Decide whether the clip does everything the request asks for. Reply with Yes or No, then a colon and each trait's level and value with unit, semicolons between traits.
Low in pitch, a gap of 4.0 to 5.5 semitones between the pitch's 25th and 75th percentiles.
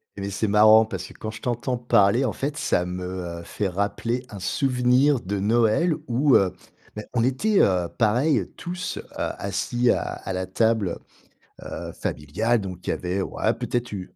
Yes: low, 110 Hz; average, 4.5 semitones